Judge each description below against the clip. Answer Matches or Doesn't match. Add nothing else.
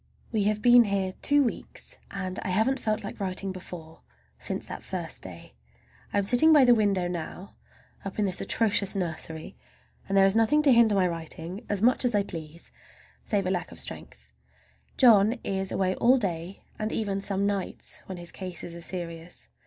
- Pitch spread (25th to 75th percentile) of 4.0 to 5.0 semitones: Doesn't match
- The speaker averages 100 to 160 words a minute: Doesn't match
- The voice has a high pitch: Matches